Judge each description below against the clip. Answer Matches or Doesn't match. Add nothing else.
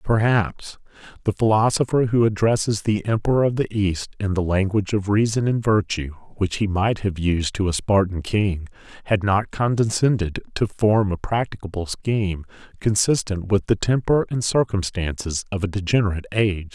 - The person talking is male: Matches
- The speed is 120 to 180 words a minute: Matches